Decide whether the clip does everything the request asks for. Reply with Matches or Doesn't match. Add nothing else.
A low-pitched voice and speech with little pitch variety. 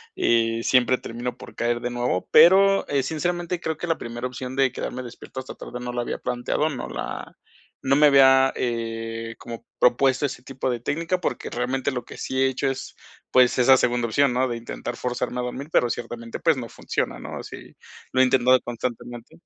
Matches